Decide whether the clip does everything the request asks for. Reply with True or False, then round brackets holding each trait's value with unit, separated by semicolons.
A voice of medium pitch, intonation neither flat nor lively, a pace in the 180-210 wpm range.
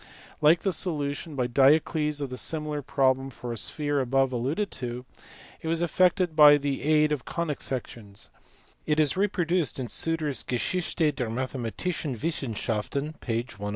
False (145 Hz; 3.9 semitones; 155 wpm)